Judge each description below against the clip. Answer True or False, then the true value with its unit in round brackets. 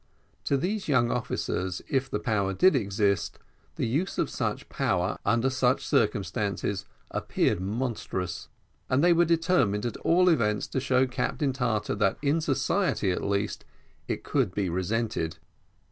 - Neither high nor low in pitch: False (115 Hz)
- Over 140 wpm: True (150 wpm)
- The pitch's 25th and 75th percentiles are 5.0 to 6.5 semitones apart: True (5.5 semitones)